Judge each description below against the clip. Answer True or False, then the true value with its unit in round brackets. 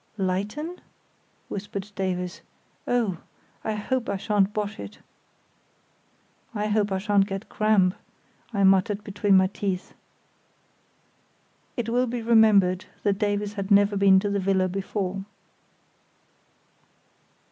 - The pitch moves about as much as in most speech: False (1.7 semitones)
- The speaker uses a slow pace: True (115 wpm)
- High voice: True (200 Hz)